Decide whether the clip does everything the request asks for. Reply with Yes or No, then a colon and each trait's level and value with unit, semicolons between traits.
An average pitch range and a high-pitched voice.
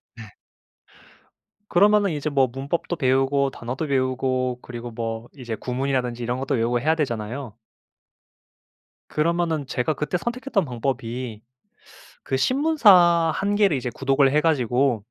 No: average, 4.8 semitones; low, 135 Hz